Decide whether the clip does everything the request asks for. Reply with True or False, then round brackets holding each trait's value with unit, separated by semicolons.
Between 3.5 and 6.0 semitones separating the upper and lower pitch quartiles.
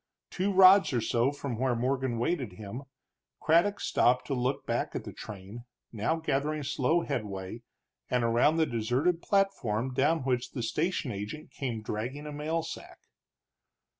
True (5.2 semitones)